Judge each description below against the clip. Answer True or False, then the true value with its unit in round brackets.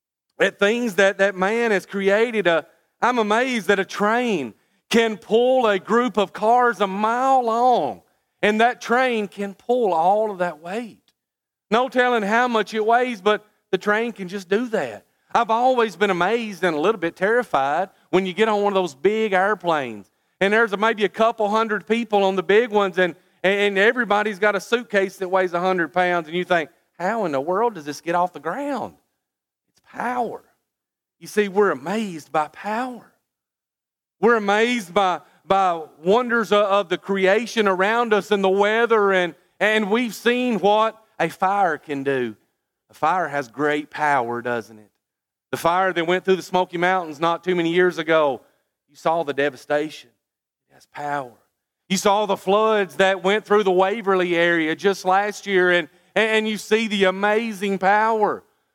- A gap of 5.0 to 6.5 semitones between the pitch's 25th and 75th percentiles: False (3.6 semitones)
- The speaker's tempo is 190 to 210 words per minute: False (175 wpm)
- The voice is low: False (200 Hz)